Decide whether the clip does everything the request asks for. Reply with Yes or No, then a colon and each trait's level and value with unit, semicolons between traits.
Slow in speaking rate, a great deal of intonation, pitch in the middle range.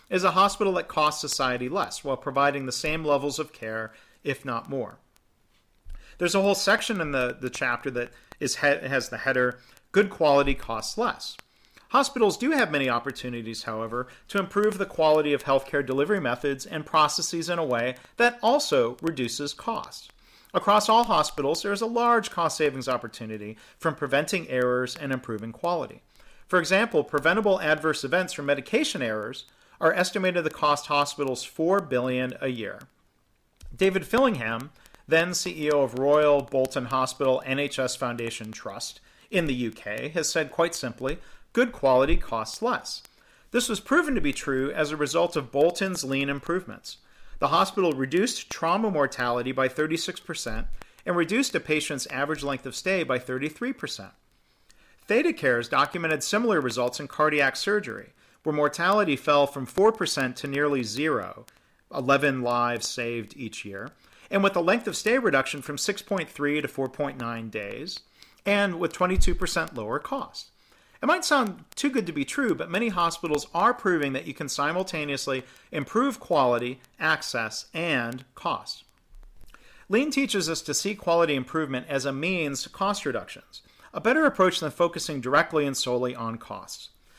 No: average, 155 wpm; wide, 6.2 semitones; medium, 145 Hz